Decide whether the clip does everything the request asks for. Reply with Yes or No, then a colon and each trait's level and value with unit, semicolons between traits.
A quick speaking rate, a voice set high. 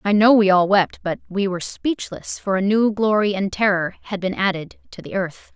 Yes: fast, 225 wpm; high, 195 Hz